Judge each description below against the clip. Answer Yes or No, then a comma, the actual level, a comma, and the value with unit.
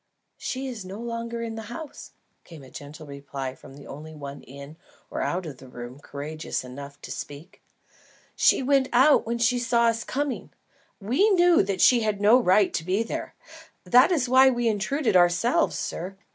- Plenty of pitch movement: Yes, wide, 8.7 semitones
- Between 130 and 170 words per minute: No, average, 185 wpm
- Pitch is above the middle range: Yes, high, 205 Hz